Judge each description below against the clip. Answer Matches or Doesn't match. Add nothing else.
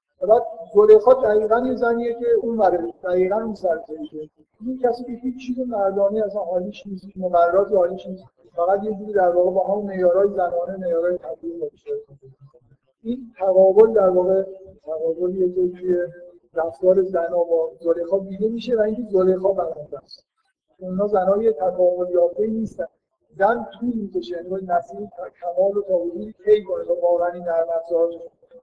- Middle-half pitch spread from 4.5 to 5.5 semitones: Doesn't match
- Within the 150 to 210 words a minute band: Matches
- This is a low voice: Doesn't match